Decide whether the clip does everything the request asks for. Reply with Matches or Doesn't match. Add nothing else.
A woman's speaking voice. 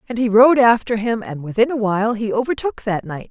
Matches